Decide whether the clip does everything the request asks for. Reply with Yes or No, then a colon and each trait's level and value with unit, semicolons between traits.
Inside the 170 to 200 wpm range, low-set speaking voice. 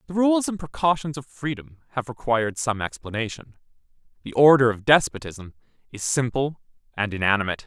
No: average, 140 wpm; low, 130 Hz